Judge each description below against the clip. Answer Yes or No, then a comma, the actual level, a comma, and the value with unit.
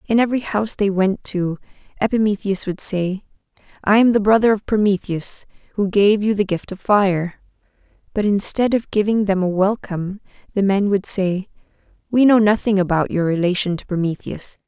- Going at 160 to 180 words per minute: Yes, average, 170 wpm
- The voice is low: No, high, 200 Hz